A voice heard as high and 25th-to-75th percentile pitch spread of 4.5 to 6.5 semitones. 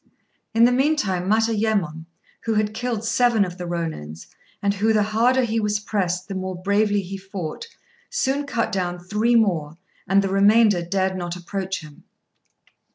No: high, 200 Hz; average, 3.7 semitones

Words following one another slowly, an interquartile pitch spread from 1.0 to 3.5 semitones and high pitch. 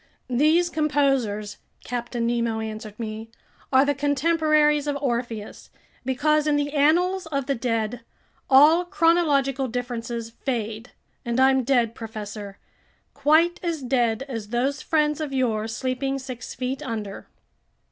No: slow, 125 wpm; average, 4.2 semitones; very high, 260 Hz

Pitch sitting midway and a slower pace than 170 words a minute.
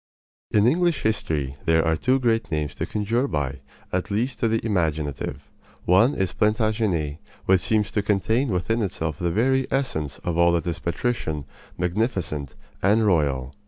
No: very low, 95 Hz; average, 160 wpm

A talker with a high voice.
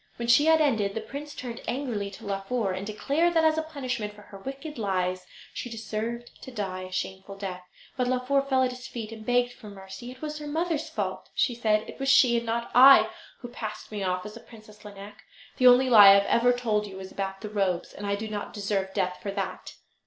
Yes: high, 225 Hz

